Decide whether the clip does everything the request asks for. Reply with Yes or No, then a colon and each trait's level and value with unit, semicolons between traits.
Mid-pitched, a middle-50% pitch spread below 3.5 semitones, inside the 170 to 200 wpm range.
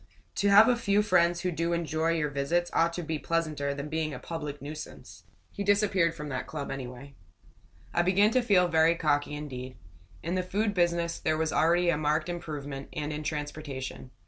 Yes: medium, 160 Hz; average, 2.9 semitones; average, 190 wpm